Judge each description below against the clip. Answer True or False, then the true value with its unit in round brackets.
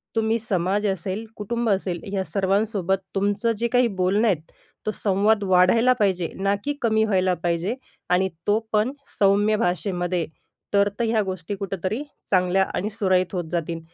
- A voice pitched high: True (195 Hz)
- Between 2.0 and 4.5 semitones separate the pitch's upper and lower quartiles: True (2.7 semitones)